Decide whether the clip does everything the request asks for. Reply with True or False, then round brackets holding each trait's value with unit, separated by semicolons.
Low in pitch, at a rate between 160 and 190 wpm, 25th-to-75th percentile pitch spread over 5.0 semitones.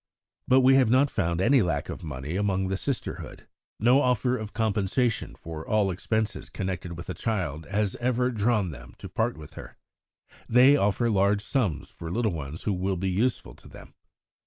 True (100 Hz; 180 wpm; 5.4 semitones)